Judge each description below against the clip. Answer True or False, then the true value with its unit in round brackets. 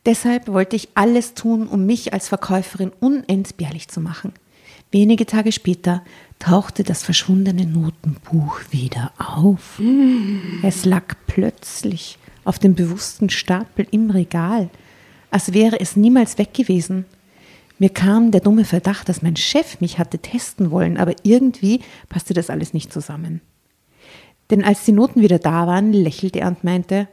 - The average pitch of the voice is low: False (190 Hz)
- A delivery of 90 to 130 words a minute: False (145 wpm)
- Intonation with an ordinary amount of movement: True (3.5 semitones)